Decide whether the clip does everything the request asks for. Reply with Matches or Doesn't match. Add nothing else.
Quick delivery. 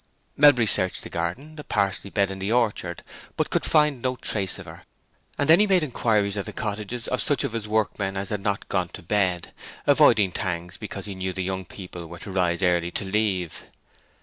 Matches